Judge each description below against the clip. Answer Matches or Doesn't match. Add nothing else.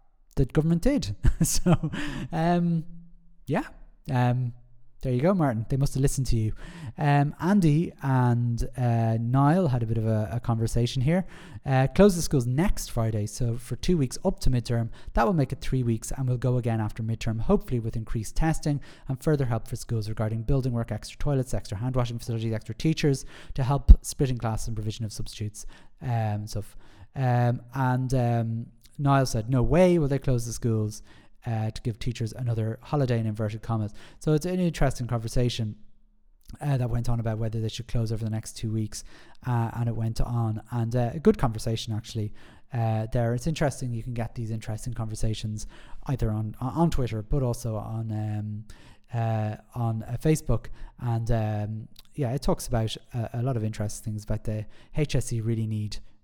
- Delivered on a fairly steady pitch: Doesn't match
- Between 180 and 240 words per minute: Matches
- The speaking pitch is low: Matches